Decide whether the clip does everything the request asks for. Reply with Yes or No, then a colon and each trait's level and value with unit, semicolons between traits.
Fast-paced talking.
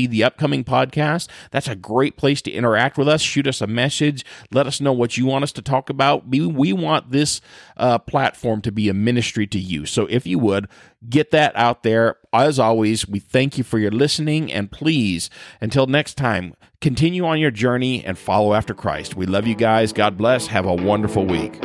Yes: fast, 210 wpm